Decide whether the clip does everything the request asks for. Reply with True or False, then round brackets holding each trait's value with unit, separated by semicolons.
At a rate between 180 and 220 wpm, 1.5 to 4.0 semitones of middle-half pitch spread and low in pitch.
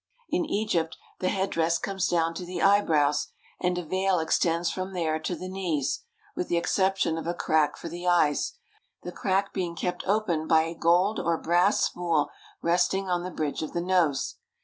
False (185 wpm; 2.4 semitones; 175 Hz)